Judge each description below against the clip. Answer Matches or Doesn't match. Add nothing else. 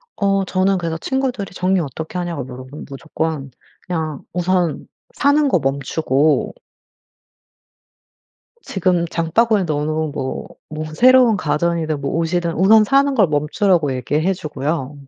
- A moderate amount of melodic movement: Matches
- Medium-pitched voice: Matches